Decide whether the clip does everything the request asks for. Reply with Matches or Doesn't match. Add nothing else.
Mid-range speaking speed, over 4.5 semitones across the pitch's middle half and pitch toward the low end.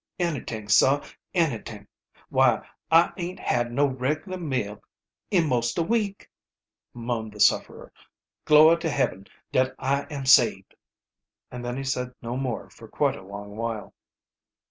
Matches